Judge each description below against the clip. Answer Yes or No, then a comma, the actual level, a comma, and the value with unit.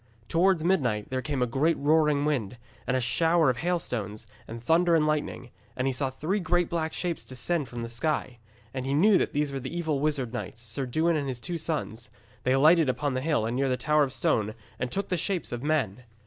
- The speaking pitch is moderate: Yes, medium, 145 Hz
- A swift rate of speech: Yes, fast, 220 wpm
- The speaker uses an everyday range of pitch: Yes, average, 4.5 semitones